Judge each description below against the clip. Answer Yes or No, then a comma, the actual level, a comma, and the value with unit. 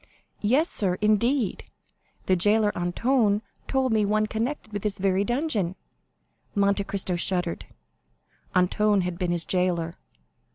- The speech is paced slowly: Yes, slow, 125 wpm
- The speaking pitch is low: No, high, 205 Hz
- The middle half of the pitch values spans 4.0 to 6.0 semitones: No, average, 3.2 semitones